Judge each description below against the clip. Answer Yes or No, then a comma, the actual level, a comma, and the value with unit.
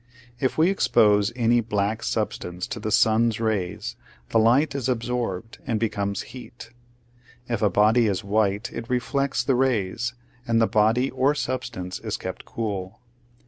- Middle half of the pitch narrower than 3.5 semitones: Yes, average, 3.0 semitones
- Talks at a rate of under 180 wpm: Yes, average, 150 wpm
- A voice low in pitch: Yes, low, 115 Hz